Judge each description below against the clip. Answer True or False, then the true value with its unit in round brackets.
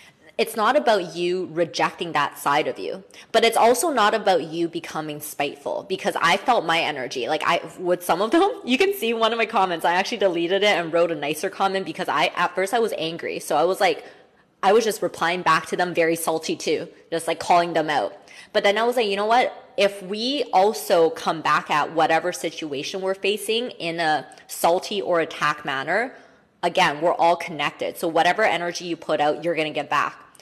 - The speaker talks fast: True (215 wpm)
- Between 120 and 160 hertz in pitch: False (180 Hz)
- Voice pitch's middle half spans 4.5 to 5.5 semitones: True (5.1 semitones)